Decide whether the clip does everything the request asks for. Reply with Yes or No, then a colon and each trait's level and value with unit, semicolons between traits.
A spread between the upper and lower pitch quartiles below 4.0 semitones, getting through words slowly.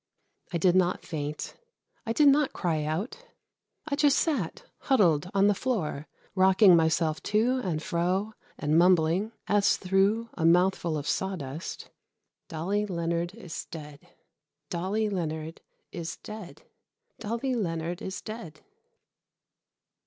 No: average, 4.5 semitones; slow, 125 wpm